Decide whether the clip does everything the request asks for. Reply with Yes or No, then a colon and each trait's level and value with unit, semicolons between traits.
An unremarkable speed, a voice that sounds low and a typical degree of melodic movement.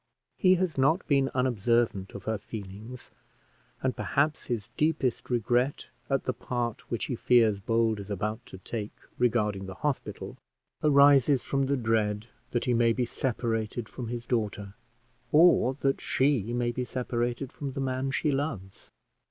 Yes: average, 155 wpm; low, 120 Hz; average, 3.5 semitones